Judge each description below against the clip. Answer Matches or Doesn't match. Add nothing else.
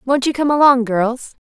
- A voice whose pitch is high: Matches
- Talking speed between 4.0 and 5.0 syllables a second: Matches